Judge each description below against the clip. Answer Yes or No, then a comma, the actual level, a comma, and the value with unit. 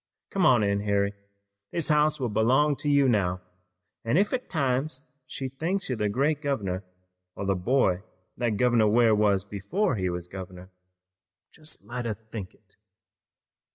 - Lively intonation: Yes, wide, 6.0 semitones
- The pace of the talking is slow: No, average, 160 wpm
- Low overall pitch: Yes, low, 120 Hz